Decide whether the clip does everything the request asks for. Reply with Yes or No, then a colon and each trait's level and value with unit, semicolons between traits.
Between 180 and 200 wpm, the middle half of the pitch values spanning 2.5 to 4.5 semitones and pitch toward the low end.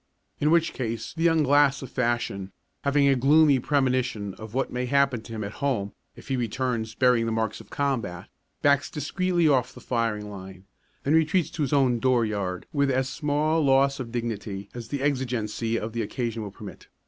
Yes: average, 190 wpm; average, 4.1 semitones; low, 125 Hz